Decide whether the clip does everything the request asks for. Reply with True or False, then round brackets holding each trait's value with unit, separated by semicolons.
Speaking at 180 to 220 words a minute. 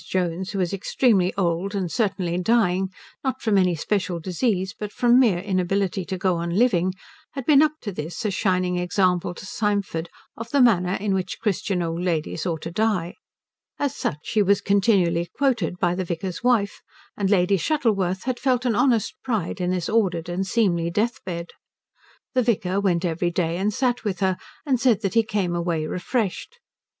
True (185 wpm)